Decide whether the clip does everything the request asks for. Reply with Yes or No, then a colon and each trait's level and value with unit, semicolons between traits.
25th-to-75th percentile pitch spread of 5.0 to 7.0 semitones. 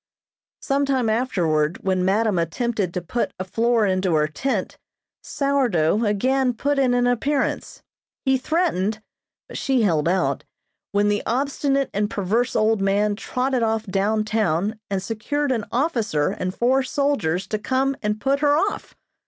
Yes: wide, 5.4 semitones